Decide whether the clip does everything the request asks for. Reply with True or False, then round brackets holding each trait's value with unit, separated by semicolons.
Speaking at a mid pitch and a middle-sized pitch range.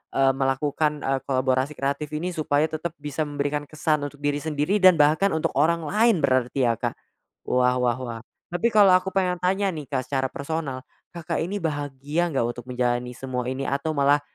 True (145 Hz; 3.5 semitones)